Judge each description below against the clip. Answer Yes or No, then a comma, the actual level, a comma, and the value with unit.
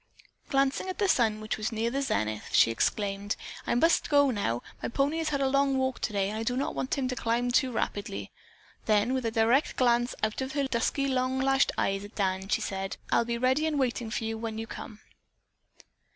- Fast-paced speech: Yes, fast, 220 wpm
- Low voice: No, high, 240 Hz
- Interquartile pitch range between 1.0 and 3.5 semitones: No, average, 3.9 semitones